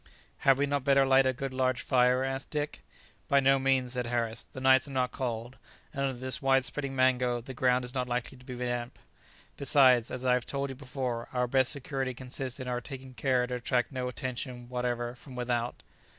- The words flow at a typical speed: No, fast, 210 wpm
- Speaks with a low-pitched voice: Yes, low, 130 Hz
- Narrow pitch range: Yes, narrow, 1.4 semitones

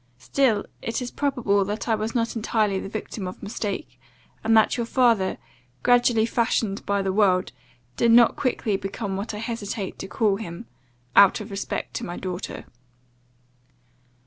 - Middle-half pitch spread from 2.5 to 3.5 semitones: Yes, average, 2.9 semitones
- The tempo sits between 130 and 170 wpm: Yes, average, 160 wpm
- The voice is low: No, high, 215 Hz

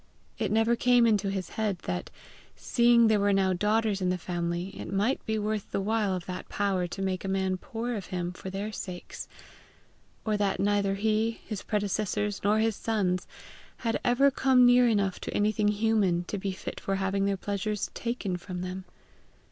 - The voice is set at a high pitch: Yes, high, 205 Hz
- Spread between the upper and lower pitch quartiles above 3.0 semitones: No, narrow, 2.6 semitones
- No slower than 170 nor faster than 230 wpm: Yes, average, 190 wpm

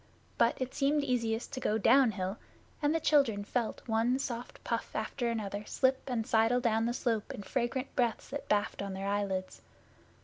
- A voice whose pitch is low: No, high, 230 Hz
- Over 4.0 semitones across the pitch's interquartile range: No, average, 3.5 semitones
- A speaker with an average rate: Yes, average, 175 wpm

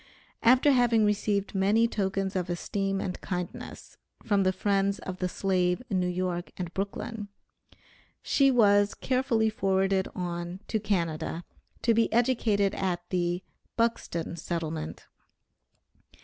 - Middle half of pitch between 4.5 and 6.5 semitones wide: No, average, 3.2 semitones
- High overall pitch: Yes, high, 195 Hz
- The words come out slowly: Yes, slow, 125 wpm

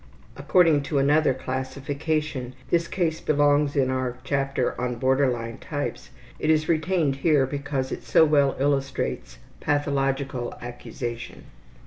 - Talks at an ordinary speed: No, slow, 125 wpm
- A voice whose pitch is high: No, medium, 140 Hz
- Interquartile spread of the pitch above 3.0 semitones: No, narrow, 2.4 semitones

